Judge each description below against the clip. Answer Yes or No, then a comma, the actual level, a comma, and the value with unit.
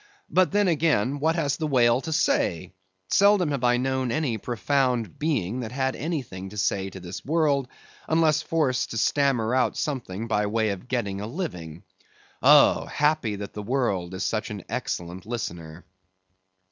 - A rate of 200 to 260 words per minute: No, average, 165 wpm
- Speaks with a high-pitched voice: No, low, 125 Hz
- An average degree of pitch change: No, wide, 6.7 semitones